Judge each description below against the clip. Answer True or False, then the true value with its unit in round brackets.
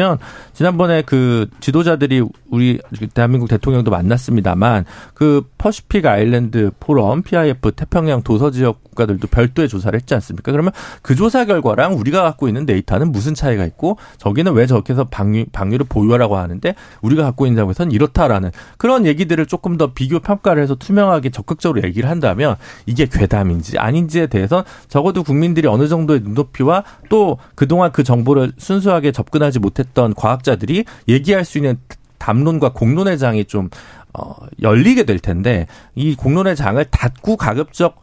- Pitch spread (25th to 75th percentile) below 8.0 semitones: True (6.3 semitones)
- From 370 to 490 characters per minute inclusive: True (375 characters per minute)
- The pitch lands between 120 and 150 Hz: True (135 Hz)